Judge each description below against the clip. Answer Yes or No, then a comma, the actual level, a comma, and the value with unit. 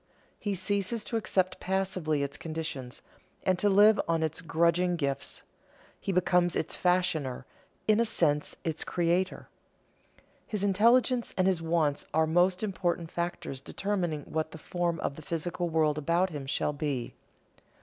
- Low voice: No, medium, 175 Hz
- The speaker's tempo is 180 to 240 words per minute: No, average, 150 wpm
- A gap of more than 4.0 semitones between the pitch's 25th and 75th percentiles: No, average, 3.1 semitones